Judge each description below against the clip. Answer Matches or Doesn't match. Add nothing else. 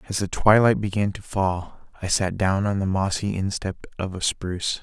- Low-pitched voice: Matches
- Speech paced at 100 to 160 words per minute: Doesn't match